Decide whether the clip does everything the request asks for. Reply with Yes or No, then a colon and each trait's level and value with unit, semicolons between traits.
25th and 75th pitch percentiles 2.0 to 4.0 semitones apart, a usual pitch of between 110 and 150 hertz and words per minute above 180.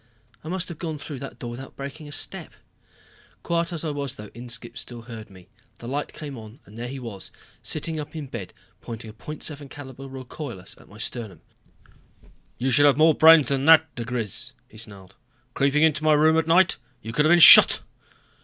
No: average, 4.8 semitones; low, 135 Hz; average, 195 wpm